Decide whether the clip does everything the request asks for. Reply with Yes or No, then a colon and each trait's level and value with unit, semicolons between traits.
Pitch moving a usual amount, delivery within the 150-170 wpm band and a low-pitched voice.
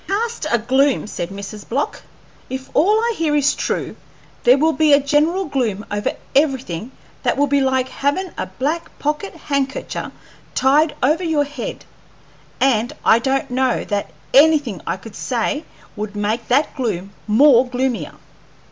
No: average, 4.4 semitones; average, 155 wpm; very high, 270 Hz